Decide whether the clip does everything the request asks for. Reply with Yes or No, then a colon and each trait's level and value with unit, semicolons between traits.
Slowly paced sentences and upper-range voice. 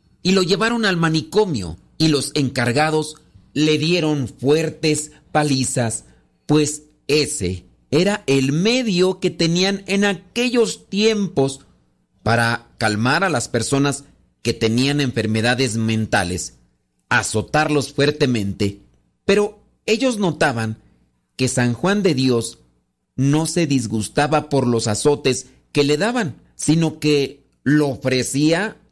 No: slow, 110 wpm; medium, 140 Hz